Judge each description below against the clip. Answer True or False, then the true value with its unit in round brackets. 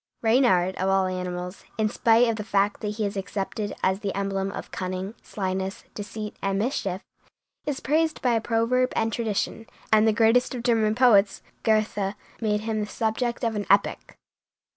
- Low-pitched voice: False (210 Hz)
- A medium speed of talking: True (170 wpm)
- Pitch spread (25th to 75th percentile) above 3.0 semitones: False (2.7 semitones)